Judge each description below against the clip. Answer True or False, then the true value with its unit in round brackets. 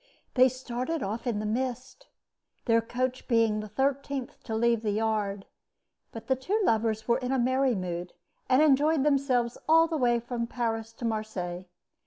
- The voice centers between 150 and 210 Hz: False (240 Hz)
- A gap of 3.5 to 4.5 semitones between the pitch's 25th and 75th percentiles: False (3.0 semitones)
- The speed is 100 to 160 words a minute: False (170 wpm)